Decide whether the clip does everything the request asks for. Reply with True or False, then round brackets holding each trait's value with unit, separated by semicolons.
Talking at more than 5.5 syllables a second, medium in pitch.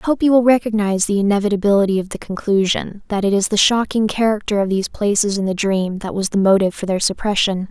False (6.5 syllables/s; 205 Hz)